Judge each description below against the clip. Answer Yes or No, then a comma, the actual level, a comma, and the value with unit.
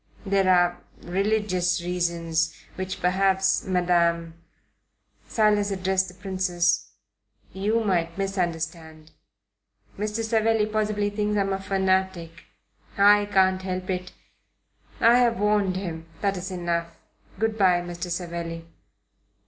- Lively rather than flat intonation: No, average, 2.7 semitones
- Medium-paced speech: No, slow, 115 wpm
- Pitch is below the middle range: No, medium, 185 Hz